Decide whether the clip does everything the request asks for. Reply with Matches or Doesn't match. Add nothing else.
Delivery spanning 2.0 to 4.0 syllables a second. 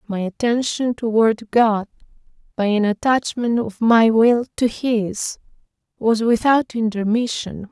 Matches